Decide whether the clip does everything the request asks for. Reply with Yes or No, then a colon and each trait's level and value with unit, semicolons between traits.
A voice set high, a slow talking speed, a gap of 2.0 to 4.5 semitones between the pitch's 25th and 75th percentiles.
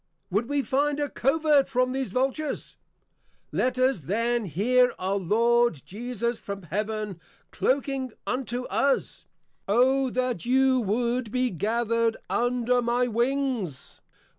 Yes: high, 245 Hz; slow, 120 wpm; average, 3.0 semitones